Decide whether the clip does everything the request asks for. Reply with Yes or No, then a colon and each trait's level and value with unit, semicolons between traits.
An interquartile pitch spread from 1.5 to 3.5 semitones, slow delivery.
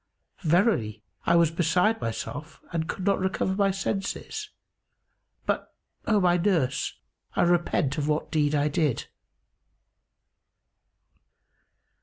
No: average, 4.4 semitones; slow, 110 wpm